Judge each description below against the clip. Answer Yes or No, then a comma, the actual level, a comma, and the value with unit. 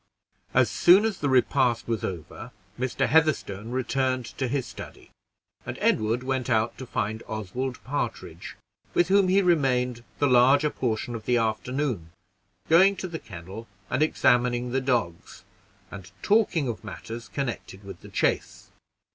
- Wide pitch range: No, average, 4.2 semitones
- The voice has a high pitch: No, low, 125 Hz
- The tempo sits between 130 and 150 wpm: Yes, average, 145 wpm